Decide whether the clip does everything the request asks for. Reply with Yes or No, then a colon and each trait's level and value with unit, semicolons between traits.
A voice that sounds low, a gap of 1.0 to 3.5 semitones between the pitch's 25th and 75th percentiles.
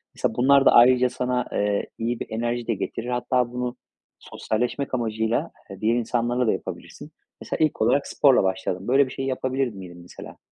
Yes: low, 120 Hz; narrow, 2.4 semitones